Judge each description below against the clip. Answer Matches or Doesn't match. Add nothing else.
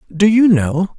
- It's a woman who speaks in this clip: Doesn't match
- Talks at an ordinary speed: Matches